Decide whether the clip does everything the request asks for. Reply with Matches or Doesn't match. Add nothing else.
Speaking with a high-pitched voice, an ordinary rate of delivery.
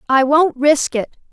Matches